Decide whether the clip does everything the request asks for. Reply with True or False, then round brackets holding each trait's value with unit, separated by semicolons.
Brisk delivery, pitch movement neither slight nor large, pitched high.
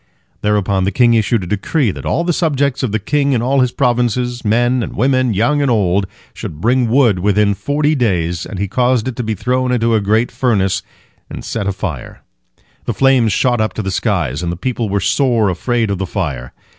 False (210 wpm; 4.4 semitones; 115 Hz)